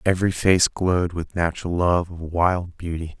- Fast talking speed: No, average, 170 wpm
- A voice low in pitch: Yes, very low, 85 Hz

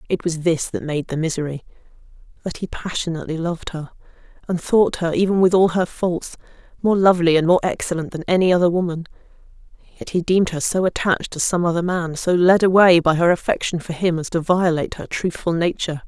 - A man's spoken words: No, female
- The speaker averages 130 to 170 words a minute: No, average, 195 wpm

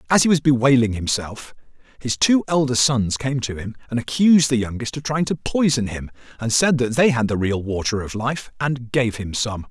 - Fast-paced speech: Yes, fast, 215 wpm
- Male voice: Yes, male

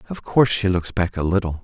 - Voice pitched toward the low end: Yes, low, 100 Hz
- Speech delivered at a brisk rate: Yes, fast, 255 wpm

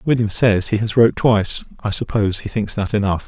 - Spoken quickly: Yes, fast, 220 wpm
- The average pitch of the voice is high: No, low, 105 Hz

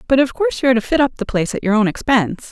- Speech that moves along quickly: Yes, fast, 335 wpm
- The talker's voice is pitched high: Yes, high, 235 Hz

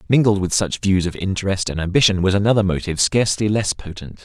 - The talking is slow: No, average, 200 wpm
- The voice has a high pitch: No, very low, 95 Hz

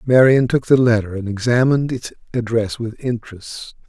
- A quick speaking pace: No, average, 155 wpm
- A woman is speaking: No, male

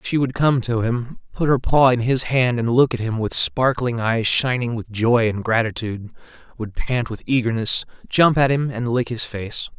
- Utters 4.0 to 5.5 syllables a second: Yes, 4.7 syllables/s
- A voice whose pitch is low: Yes, low, 120 Hz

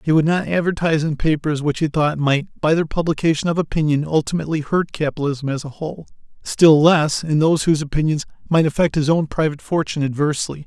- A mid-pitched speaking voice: Yes, medium, 155 Hz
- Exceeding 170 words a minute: Yes, average, 190 wpm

